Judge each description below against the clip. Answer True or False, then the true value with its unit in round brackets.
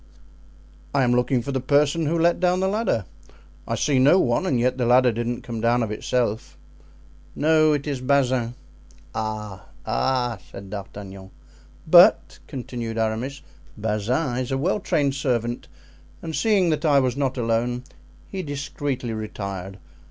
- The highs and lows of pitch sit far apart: False (4.0 semitones)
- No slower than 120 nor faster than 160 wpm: True (150 wpm)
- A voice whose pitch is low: True (125 Hz)